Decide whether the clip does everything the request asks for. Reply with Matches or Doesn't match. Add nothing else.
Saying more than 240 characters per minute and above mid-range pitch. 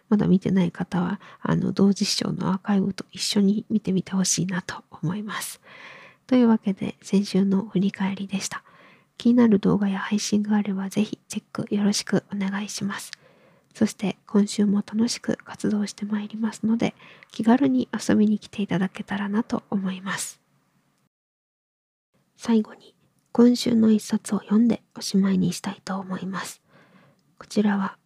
Matches